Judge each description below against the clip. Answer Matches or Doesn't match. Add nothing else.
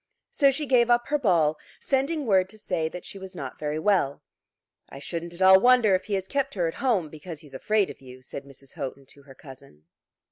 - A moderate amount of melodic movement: Doesn't match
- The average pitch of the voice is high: Doesn't match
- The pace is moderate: Doesn't match